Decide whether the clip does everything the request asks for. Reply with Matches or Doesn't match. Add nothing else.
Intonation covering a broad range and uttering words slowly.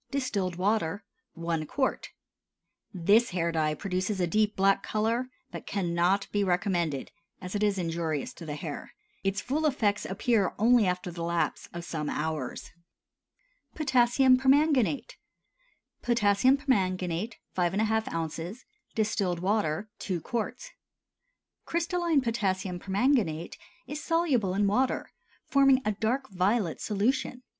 Matches